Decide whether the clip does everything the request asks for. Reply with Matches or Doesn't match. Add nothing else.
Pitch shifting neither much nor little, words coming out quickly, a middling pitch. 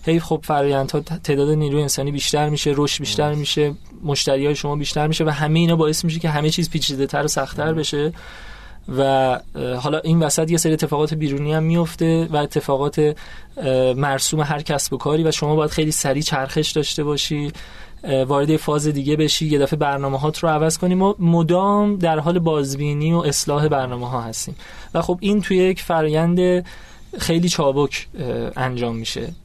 Doesn't match